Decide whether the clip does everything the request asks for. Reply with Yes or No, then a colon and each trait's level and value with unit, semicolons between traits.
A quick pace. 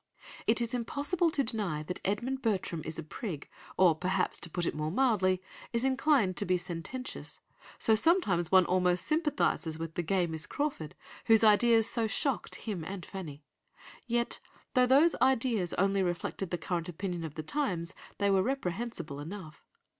No: average, 170 wpm